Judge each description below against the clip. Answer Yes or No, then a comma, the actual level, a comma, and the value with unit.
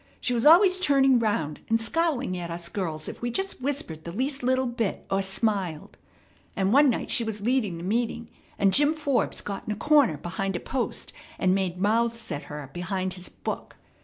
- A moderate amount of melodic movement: No, wide, 6.0 semitones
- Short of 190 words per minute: No, average, 195 wpm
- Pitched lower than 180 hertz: No, high, 220 Hz